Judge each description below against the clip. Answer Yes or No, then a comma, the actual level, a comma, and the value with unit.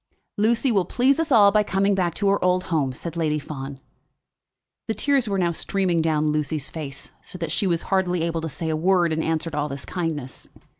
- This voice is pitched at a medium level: Yes, medium, 170 Hz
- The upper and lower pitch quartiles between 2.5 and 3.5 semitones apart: No, average, 4.1 semitones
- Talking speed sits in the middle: No, fast, 215 wpm